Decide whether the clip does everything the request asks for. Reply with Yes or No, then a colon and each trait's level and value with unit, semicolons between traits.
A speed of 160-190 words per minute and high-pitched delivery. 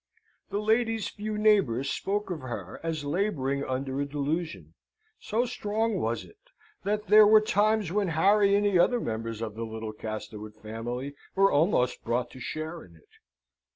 No: average, 165 wpm; medium, 160 Hz